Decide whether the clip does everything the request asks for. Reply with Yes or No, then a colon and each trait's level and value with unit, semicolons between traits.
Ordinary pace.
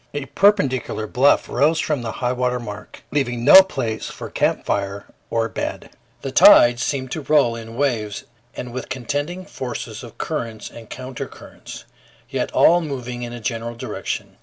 Yes: average, 160 wpm